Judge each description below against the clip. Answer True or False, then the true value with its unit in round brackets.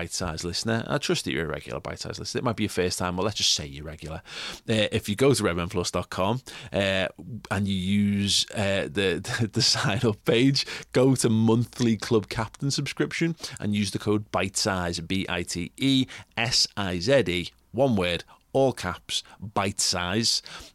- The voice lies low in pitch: True (105 Hz)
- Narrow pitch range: False (4.6 semitones)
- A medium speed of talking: True (190 wpm)